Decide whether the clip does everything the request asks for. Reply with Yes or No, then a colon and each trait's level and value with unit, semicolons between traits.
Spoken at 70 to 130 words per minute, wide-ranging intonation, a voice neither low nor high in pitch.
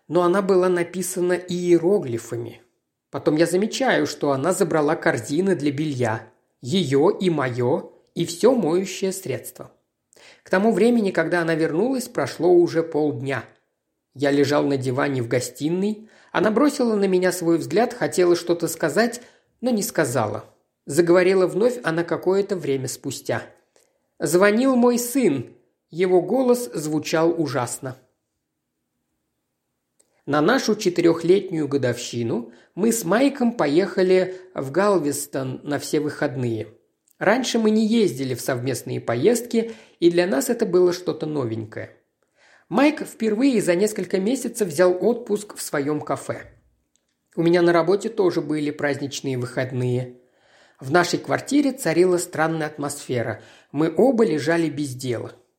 Yes: average, 125 wpm; wide, 5.7 semitones; medium, 165 Hz